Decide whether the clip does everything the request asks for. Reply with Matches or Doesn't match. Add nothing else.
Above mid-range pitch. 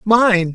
Matches